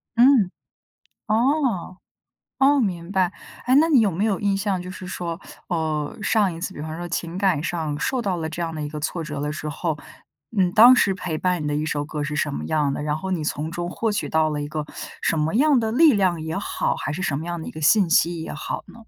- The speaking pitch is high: No, medium, 175 Hz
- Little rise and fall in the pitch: No, average, 4.5 semitones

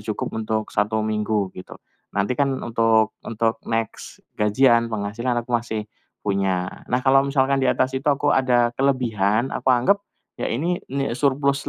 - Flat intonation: No, average, 3.6 semitones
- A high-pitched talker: No, low, 120 Hz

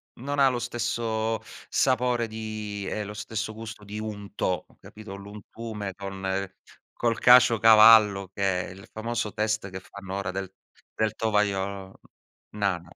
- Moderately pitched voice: No, low, 105 Hz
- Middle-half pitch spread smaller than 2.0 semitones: No, narrow, 2.4 semitones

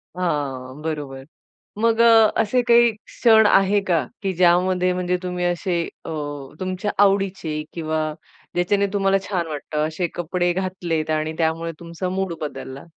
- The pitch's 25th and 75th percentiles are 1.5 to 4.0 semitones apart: Yes, average, 3.5 semitones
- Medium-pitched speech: Yes, medium, 180 Hz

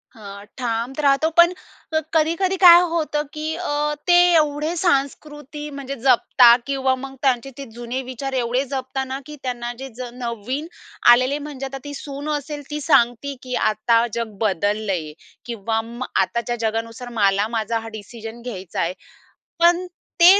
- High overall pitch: Yes, very high, 260 Hz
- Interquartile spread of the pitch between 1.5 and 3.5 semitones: No, average, 4.2 semitones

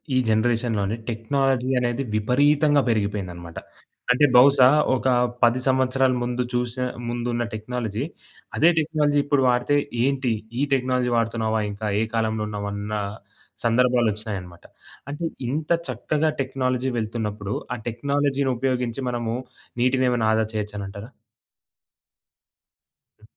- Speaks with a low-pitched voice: Yes, low, 120 Hz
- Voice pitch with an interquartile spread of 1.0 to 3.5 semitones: Yes, average, 3.2 semitones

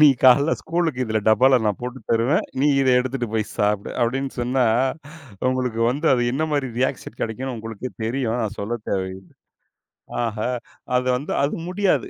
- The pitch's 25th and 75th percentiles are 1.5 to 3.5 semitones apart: Yes, average, 3.2 semitones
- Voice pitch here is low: Yes, low, 125 Hz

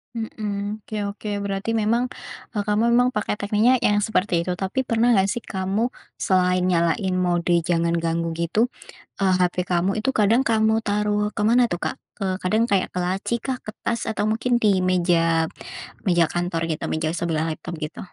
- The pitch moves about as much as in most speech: Yes, average, 3.5 semitones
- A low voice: No, high, 200 Hz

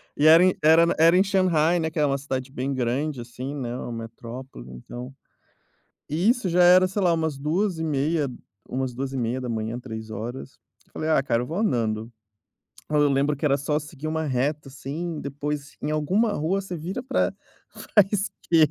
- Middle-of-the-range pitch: Yes, medium, 150 Hz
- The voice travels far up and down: No, average, 4.4 semitones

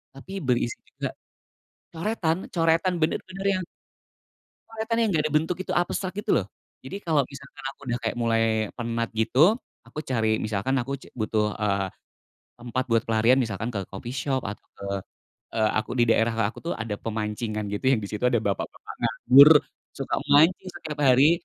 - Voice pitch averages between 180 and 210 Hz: No, low, 125 Hz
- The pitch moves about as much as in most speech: No, wide, 6.3 semitones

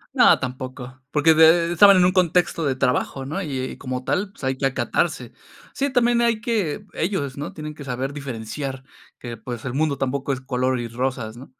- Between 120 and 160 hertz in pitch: Yes, medium, 140 Hz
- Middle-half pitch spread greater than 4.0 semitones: Yes, average, 4.6 semitones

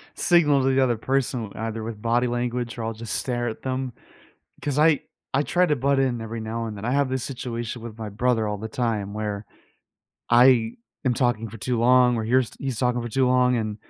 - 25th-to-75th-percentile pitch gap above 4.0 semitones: No, narrow, 2.5 semitones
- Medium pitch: No, low, 120 Hz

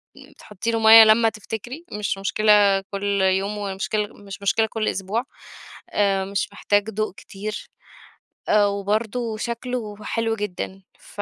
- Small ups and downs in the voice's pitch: Yes, narrow, 1.9 semitones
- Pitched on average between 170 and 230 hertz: Yes, high, 210 Hz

